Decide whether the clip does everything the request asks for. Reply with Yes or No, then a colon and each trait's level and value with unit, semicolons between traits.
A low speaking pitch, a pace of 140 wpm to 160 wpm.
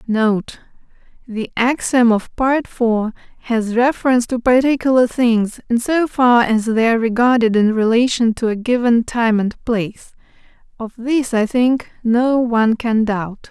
No: high, 235 Hz; average, 145 wpm